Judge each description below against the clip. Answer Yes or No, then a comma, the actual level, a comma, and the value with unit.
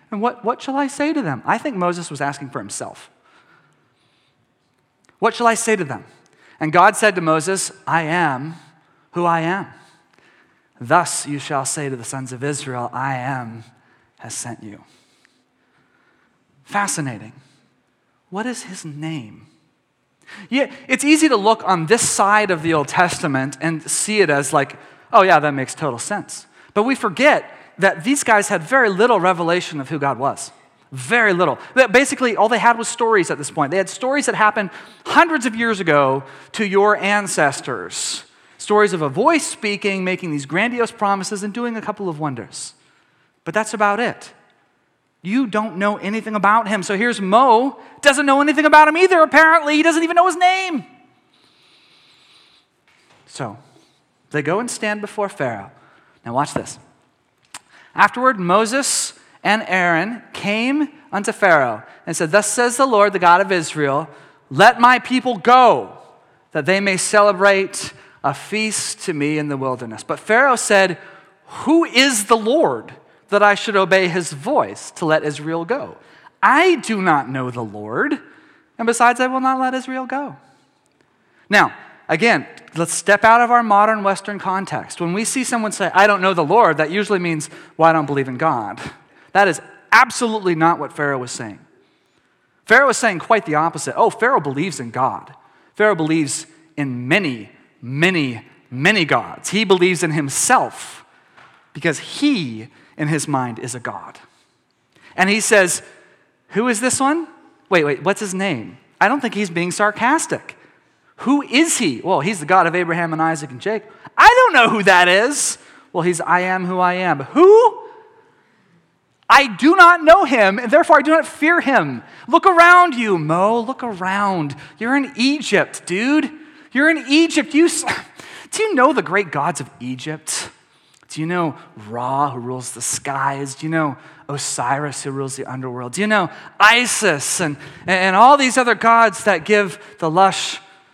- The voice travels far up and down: Yes, wide, 7.4 semitones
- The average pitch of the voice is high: Yes, high, 200 Hz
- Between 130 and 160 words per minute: No, average, 170 wpm